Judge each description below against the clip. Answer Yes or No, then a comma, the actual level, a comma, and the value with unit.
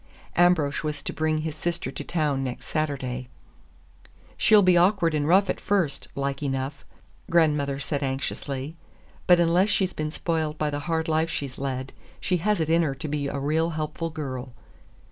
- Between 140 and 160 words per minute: No, average, 175 wpm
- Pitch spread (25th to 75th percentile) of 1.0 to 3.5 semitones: Yes, average, 3.2 semitones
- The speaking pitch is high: No, medium, 155 Hz